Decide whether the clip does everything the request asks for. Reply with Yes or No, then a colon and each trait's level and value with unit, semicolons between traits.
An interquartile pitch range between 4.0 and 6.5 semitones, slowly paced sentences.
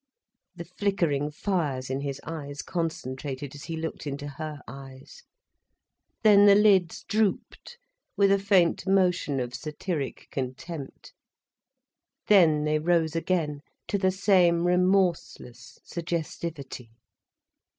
Yes: average, 4.6 semitones; slow, 110 wpm